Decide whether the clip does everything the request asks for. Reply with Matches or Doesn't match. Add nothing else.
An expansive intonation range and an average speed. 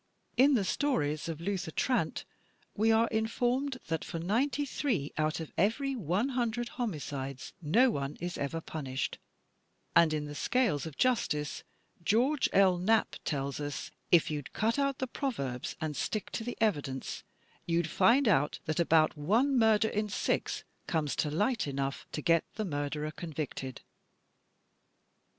Matches